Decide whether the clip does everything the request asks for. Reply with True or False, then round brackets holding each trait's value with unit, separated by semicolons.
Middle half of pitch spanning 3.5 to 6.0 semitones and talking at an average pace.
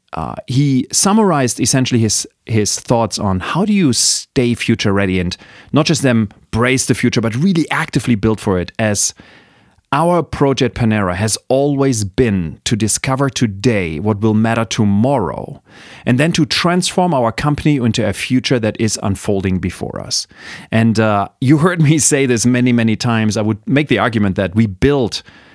True (4.3 semitones; 170 wpm)